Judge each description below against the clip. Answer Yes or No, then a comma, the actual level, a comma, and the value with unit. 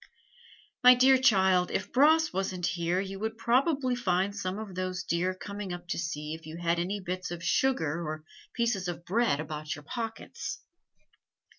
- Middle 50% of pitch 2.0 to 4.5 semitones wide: No, average, 4.9 semitones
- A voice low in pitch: No, medium, 185 Hz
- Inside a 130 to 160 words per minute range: No, average, 170 wpm